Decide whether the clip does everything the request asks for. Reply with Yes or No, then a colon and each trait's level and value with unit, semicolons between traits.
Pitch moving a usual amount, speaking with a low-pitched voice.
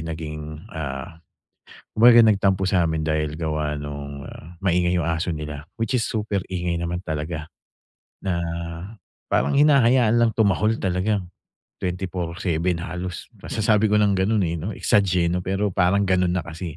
Yes: average, 4.0 semitones; very low, 90 Hz